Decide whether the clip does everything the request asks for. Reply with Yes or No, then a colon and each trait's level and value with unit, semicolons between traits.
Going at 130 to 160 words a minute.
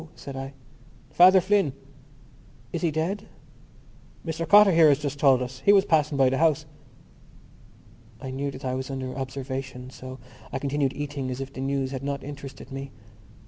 No: average, 175 wpm